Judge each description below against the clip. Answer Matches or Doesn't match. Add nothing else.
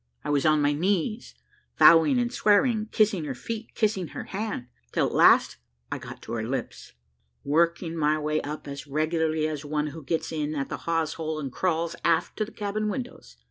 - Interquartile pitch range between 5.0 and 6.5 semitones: Matches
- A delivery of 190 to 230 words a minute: Matches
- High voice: Doesn't match